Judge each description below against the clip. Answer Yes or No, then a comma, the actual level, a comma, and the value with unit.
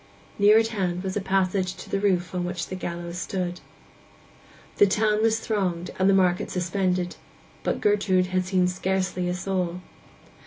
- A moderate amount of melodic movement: No, narrow, 1.7 semitones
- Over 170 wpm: No, average, 165 wpm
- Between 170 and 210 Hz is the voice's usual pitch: Yes, medium, 185 Hz